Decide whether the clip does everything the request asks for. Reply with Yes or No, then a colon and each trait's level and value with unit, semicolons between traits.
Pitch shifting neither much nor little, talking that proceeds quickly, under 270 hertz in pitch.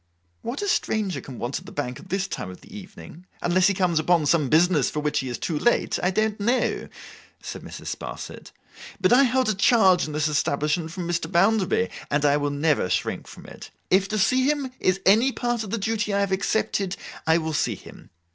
No: wide, 5.8 semitones; fast, 220 wpm; medium, 185 Hz